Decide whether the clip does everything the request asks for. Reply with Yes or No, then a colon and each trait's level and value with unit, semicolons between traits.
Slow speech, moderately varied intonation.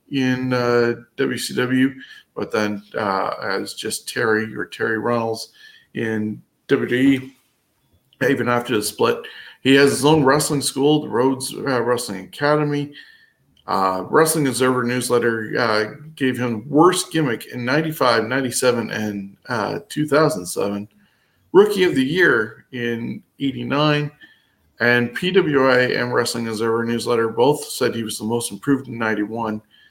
Yes: slow, 130 wpm; average, 3.9 semitones